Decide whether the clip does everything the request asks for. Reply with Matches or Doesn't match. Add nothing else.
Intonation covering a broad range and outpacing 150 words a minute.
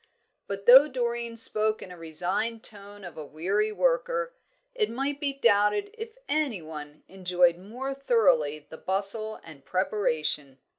Doesn't match